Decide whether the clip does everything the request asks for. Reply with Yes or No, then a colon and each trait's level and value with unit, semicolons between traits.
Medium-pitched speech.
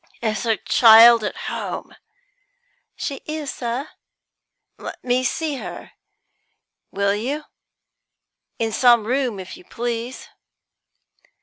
No: high, 240 Hz